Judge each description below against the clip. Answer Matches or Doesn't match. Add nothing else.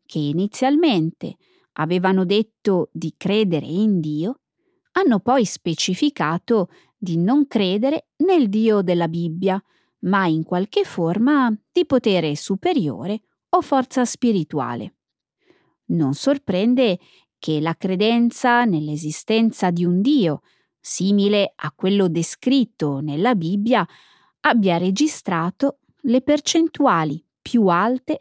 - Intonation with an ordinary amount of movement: Doesn't match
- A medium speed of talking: Doesn't match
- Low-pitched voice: Doesn't match